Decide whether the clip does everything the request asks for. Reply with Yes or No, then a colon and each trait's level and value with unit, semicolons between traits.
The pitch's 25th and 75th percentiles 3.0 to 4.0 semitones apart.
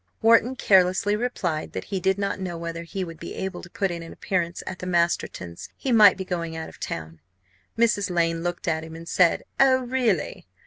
Yes: average, 3.4 semitones